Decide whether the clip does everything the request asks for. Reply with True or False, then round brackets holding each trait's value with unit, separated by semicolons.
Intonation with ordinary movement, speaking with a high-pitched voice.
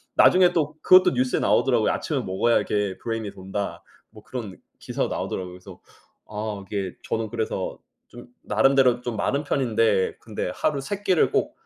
False (5.0 semitones; 115 Hz)